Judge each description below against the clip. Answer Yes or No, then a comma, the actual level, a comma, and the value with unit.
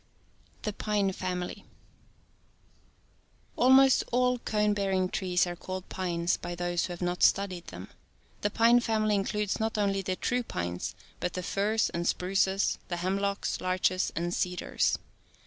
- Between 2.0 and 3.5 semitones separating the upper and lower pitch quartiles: Yes, average, 2.8 semitones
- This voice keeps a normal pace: Yes, average, 145 wpm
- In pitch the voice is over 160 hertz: Yes, high, 190 Hz